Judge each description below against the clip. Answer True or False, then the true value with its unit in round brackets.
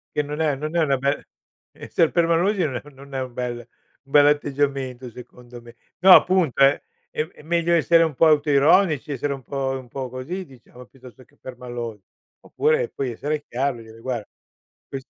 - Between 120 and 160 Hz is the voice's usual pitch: True (140 Hz)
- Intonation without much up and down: False (3.8 semitones)